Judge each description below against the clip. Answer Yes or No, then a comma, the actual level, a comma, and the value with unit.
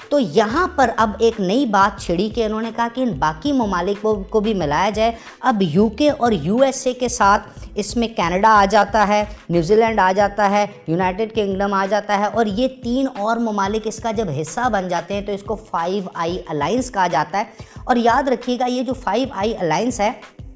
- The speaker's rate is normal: No, fast, 220 wpm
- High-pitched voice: Yes, high, 215 Hz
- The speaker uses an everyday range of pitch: Yes, average, 3.1 semitones